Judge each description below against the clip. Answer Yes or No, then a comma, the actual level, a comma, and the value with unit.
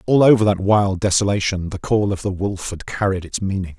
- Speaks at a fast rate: Yes, fast, 220 wpm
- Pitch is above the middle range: No, low, 100 Hz